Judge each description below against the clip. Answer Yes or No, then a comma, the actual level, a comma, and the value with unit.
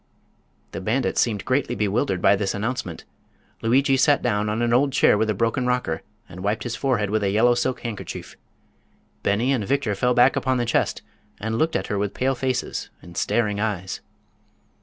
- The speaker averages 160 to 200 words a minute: Yes, average, 185 wpm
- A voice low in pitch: Yes, low, 115 Hz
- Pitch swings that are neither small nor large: Yes, average, 3.7 semitones